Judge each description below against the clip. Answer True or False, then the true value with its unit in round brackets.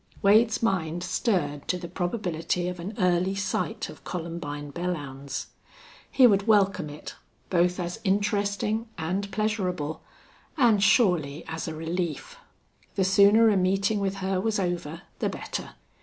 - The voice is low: False (185 Hz)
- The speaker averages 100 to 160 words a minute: True (140 wpm)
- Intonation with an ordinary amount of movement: True (3.1 semitones)